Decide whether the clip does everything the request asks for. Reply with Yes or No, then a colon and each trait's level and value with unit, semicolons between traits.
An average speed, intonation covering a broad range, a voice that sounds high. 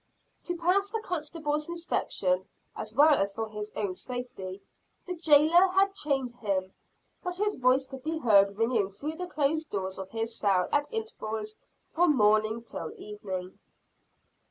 Yes: average, 155 wpm; wide, 7.6 semitones; very high, 255 Hz